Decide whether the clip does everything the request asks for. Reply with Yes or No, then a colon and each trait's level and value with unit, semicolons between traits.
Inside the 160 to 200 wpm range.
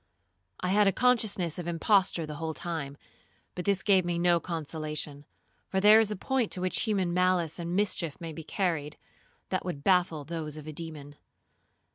Yes: average, 180 wpm